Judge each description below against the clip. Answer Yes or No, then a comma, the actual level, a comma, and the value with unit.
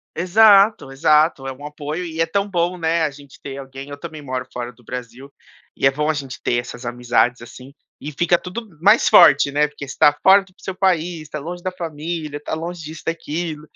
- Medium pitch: Yes, medium, 150 Hz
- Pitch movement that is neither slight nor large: Yes, average, 4.1 semitones